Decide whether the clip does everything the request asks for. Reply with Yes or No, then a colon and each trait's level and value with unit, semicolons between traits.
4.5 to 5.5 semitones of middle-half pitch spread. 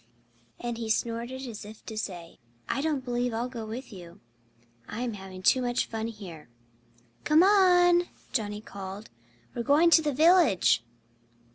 Yes: average, 5.2 semitones